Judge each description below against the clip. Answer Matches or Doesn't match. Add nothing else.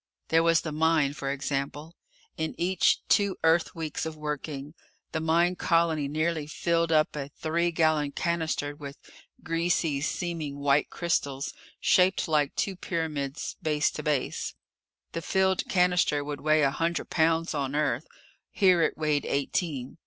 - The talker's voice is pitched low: Doesn't match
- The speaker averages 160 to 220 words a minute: Doesn't match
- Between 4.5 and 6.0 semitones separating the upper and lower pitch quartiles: Doesn't match